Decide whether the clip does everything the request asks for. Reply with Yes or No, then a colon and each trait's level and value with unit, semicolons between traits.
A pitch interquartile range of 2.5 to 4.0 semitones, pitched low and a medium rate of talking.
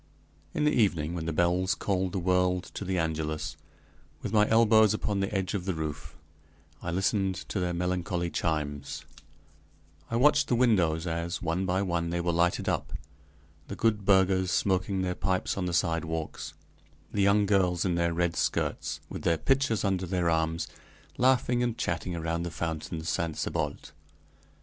Yes: average, 3.0 semitones; very low, 90 Hz; average, 170 wpm